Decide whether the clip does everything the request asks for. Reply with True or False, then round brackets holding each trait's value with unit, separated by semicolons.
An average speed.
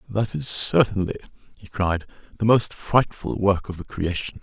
True (165 wpm)